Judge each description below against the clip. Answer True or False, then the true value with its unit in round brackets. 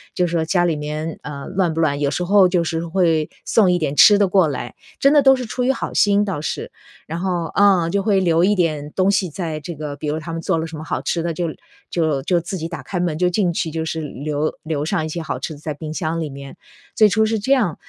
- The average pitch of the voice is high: False (165 Hz)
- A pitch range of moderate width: True (3.6 semitones)